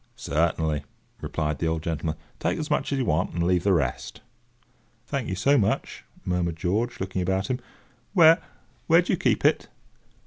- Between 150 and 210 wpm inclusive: Yes, average, 170 wpm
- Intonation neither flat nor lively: No, wide, 6.7 semitones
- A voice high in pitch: No, very low, 90 Hz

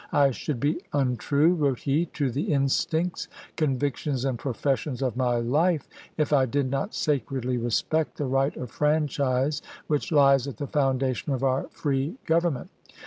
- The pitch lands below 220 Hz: Yes, medium, 140 Hz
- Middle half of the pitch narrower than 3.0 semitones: Yes, narrow, 2.5 semitones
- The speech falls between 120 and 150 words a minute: No, average, 160 wpm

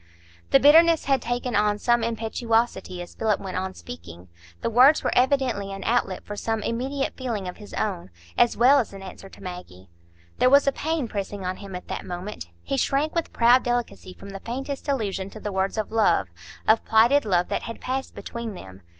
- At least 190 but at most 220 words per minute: Yes, average, 200 wpm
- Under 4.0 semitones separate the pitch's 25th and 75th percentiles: No, average, 4.8 semitones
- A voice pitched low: No, high, 220 Hz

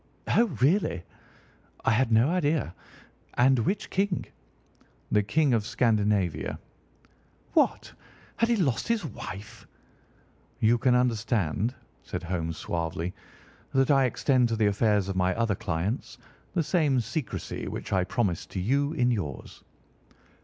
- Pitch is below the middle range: Yes, low, 115 Hz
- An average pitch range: No, wide, 5.8 semitones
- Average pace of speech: No, slow, 130 wpm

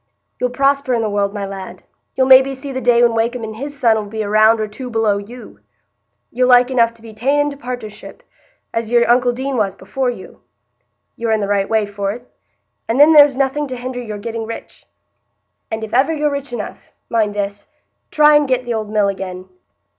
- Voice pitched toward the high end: Yes, high, 230 Hz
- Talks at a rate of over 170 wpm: Yes, average, 200 wpm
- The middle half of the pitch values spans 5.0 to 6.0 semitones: No, average, 3.7 semitones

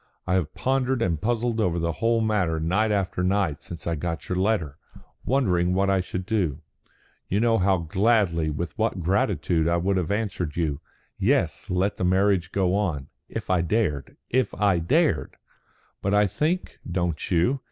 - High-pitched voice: No, very low, 95 Hz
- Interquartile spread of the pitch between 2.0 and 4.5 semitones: Yes, average, 4.0 semitones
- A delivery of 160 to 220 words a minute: Yes, average, 175 wpm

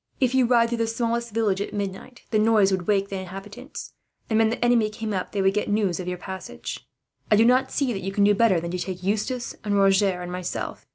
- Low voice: No, high, 205 Hz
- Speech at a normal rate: No, fast, 240 wpm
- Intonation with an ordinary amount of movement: Yes, average, 3.3 semitones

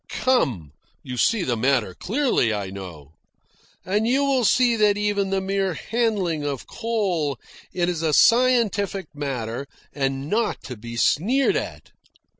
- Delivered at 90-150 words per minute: Yes, average, 140 wpm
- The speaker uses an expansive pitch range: Yes, wide, 9.0 semitones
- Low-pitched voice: No, medium, 180 Hz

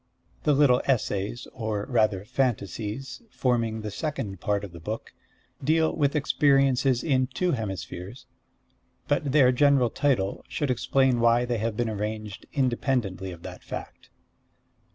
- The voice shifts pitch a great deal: No, average, 4.4 semitones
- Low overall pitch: Yes, low, 120 Hz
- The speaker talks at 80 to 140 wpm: Yes, slow, 135 wpm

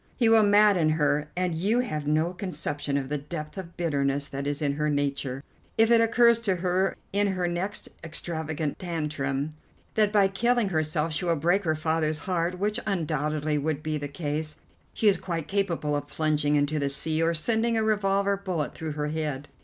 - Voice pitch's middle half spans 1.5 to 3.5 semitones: No, average, 4.7 semitones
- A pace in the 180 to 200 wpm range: Yes, average, 190 wpm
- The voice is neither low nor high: Yes, medium, 160 Hz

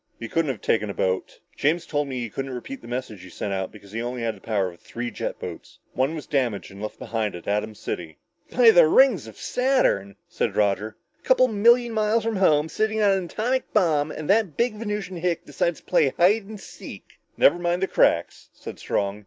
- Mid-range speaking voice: Yes, medium, 150 Hz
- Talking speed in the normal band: No, fast, 220 wpm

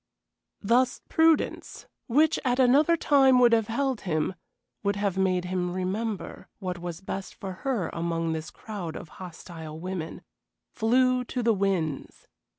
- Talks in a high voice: Yes, high, 200 Hz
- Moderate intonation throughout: No, wide, 6.0 semitones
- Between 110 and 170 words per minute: Yes, average, 145 wpm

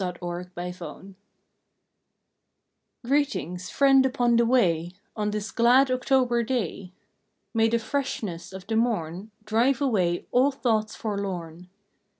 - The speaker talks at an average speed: No, slow, 125 wpm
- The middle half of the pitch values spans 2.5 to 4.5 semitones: No, wide, 5.6 semitones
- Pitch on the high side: Yes, high, 220 Hz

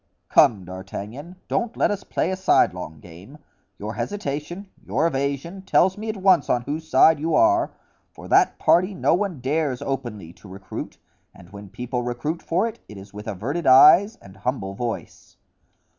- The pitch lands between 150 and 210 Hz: No, medium, 140 Hz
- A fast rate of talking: No, average, 170 wpm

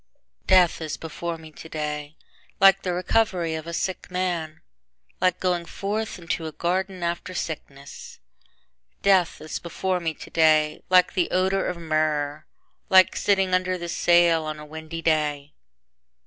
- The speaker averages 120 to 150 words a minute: Yes, average, 145 wpm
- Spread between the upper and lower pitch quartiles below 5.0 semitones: Yes, average, 2.8 semitones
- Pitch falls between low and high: Yes, medium, 170 Hz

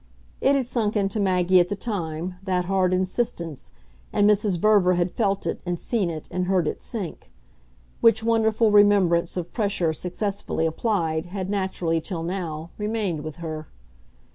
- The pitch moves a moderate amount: Yes, average, 3.4 semitones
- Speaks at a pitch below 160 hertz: No, medium, 185 Hz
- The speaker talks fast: No, average, 160 wpm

